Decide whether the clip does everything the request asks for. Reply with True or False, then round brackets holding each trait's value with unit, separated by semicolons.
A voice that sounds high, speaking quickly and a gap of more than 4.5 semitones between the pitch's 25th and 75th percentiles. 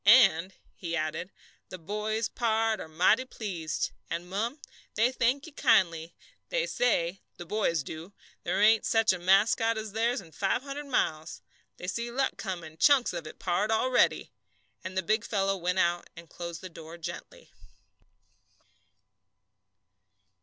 False (195 Hz; 150 wpm; 4.9 semitones)